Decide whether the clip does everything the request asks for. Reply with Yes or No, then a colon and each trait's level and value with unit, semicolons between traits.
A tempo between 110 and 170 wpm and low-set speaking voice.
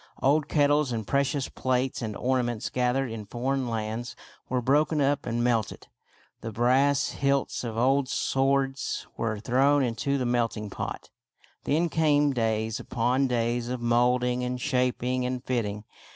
Yes: average, 150 wpm; low, 125 Hz